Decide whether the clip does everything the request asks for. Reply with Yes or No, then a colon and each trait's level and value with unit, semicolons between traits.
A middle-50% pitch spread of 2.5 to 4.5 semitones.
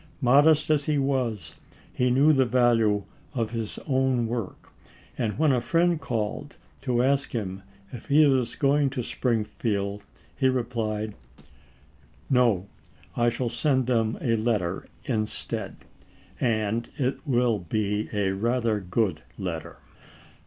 Yes: average, 3.5 semitones